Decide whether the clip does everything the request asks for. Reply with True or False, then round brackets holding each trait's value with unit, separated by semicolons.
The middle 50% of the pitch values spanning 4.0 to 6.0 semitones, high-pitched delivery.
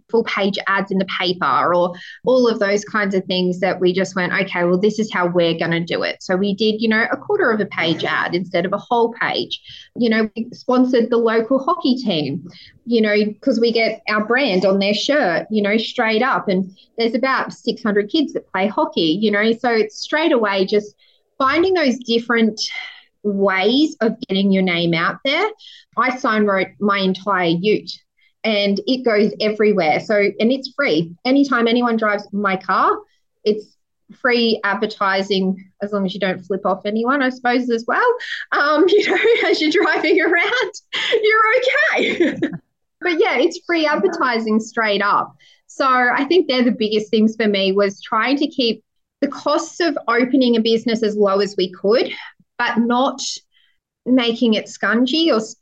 True (5.0 semitones; 225 Hz)